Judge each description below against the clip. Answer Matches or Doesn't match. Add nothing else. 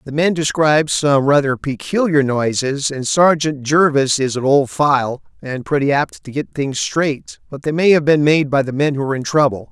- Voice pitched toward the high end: Doesn't match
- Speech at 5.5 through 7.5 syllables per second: Doesn't match